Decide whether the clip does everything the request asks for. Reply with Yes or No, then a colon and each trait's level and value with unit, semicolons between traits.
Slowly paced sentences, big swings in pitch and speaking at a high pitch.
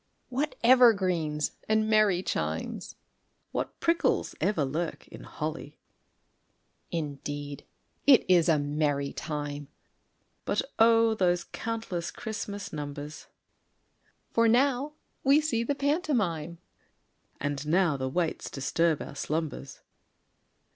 No: slow, 105 wpm; wide, 7.4 semitones; medium, 175 Hz